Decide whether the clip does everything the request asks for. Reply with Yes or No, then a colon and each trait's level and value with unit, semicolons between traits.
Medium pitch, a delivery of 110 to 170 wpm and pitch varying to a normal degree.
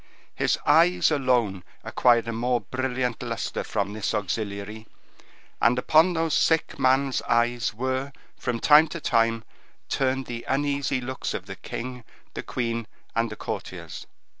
No: low, 125 Hz; average, 140 wpm; average, 3.0 semitones